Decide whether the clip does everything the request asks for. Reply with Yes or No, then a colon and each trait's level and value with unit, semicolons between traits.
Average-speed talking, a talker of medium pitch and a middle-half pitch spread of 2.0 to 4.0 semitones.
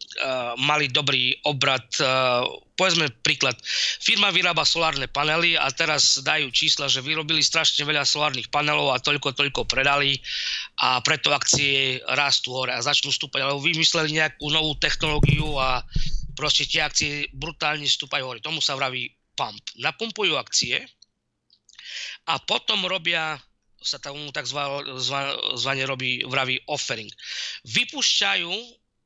Yes: average, 130 wpm; medium, 145 Hz; average, 2.7 semitones